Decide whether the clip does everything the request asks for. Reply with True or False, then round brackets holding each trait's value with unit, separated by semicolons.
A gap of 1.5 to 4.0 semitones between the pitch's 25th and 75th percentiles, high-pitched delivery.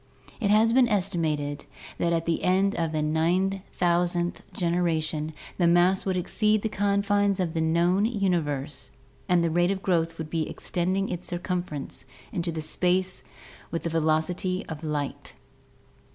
False (2.8 semitones; 175 Hz)